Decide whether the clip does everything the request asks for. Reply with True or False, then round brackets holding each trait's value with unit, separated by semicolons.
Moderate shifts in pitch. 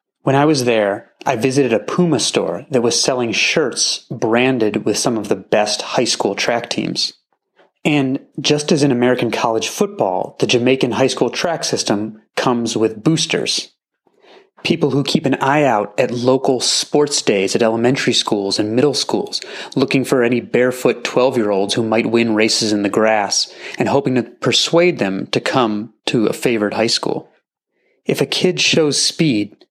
True (4.9 semitones)